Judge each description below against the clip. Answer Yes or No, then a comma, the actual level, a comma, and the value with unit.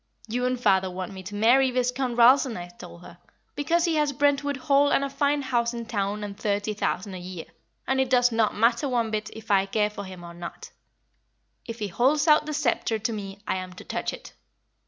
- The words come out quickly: Yes, fast, 220 wpm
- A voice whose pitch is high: Yes, high, 230 Hz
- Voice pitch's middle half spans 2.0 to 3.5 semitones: No, average, 5.1 semitones